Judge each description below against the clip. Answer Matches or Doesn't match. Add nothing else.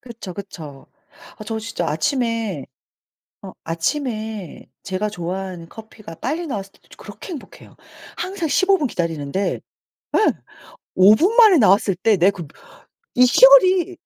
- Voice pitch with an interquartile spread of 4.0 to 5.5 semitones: Doesn't match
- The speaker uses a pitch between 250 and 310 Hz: Doesn't match